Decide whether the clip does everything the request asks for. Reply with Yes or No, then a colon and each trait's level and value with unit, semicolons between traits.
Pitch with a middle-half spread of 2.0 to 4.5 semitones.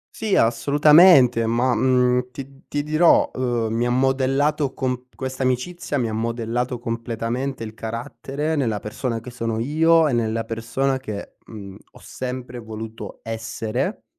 Yes: average, 2.9 semitones